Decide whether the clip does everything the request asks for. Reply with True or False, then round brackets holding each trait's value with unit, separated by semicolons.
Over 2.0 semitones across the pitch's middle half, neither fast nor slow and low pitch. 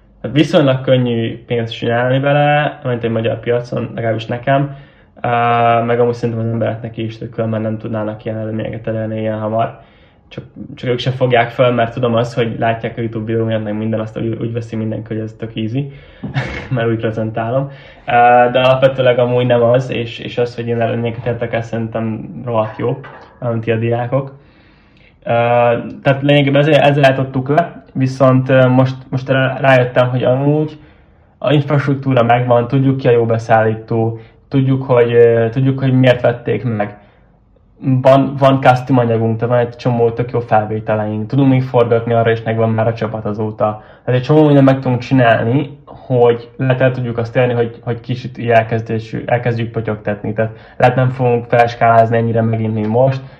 False (2.4 semitones; 170 wpm; 120 Hz)